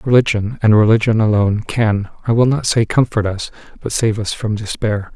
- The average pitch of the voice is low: Yes, low, 110 Hz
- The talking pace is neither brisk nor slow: Yes, average, 165 wpm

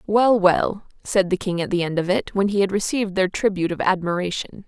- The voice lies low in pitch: No, high, 190 Hz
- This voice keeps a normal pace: No, fast, 230 wpm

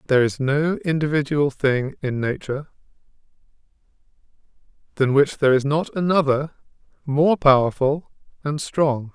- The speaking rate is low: Yes, slow, 110 wpm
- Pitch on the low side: No, medium, 145 Hz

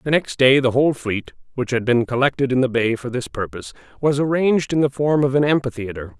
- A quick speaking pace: Yes, fast, 230 wpm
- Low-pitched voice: Yes, low, 130 Hz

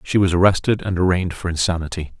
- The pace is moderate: Yes, average, 190 wpm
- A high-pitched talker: No, very low, 90 Hz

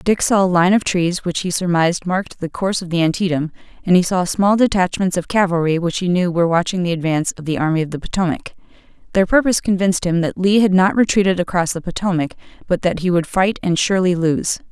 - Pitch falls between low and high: Yes, medium, 180 Hz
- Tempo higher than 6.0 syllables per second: Yes, 6.3 syllables/s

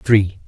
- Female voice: No, male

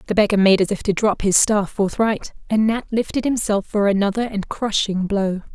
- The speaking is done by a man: No, female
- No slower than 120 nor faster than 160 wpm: No, fast, 205 wpm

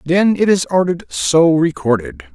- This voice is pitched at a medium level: Yes, medium, 155 Hz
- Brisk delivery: No, average, 155 wpm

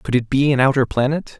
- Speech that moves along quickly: Yes, fast, 260 wpm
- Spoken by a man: Yes, male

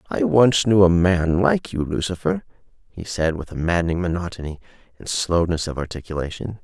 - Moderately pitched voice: No, very low, 90 Hz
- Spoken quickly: No, average, 165 wpm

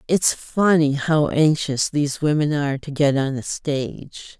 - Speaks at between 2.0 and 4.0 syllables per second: No, 4.3 syllables/s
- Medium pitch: Yes, medium, 145 Hz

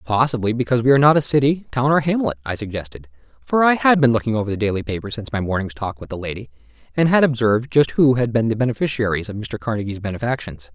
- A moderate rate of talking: No, fast, 230 wpm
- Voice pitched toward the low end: Yes, low, 120 Hz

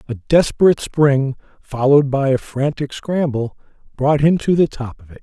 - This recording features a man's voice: Yes, male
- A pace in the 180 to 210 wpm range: No, average, 170 wpm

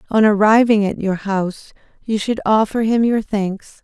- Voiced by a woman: Yes, female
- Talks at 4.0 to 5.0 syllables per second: Yes, 4.6 syllables/s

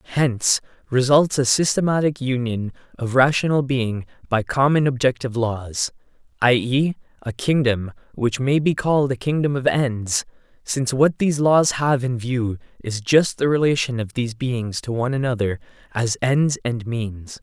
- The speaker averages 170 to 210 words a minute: No, average, 155 wpm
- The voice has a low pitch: Yes, low, 130 Hz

